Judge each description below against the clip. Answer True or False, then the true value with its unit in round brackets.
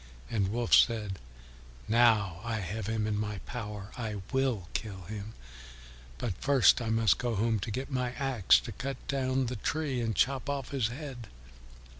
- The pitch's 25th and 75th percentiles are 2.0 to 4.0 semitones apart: True (3.4 semitones)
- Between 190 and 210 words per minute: False (175 wpm)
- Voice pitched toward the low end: True (115 Hz)